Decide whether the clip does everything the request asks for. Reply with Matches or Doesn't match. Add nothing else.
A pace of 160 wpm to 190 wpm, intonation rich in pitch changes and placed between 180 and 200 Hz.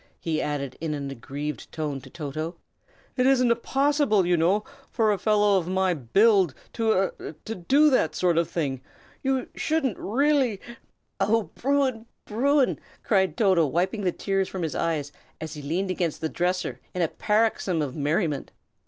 Matches